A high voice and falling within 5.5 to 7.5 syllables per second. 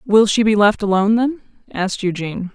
Yes: high, 210 Hz; 6.1 syllables/s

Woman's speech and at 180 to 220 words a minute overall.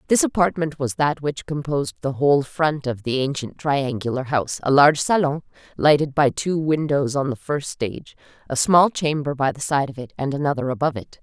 Yes: female; average, 200 wpm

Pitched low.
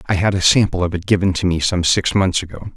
Yes: very low, 95 Hz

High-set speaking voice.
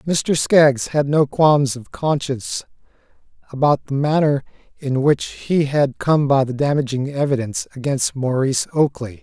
No: medium, 140 Hz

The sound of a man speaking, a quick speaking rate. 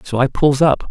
Yes: male; fast, 265 wpm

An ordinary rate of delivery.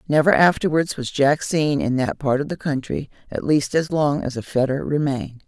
No: fast, 210 wpm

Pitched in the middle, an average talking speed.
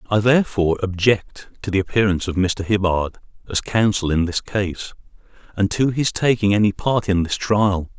No: low, 100 Hz; average, 175 wpm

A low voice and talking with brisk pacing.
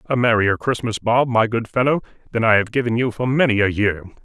Yes: low, 115 Hz; fast, 225 wpm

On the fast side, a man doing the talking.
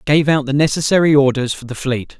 Yes: fast, 220 wpm; male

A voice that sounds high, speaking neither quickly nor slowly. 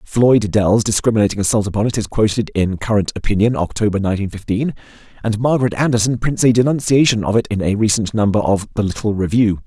No: low, 110 Hz; average, 185 wpm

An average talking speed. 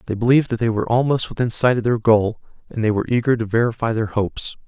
No: fast, 245 wpm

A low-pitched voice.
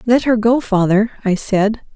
No: high, 215 Hz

